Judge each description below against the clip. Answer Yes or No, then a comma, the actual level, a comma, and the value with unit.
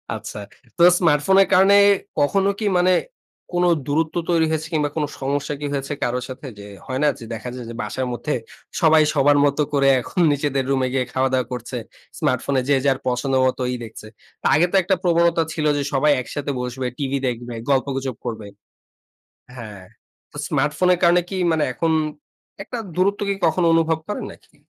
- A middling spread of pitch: Yes, average, 4.2 semitones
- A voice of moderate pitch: Yes, medium, 145 Hz